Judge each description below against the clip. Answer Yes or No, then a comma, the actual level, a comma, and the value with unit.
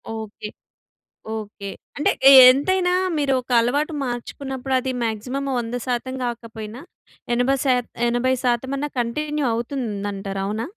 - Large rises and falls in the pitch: No, average, 3.2 semitones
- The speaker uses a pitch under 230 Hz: No, high, 245 Hz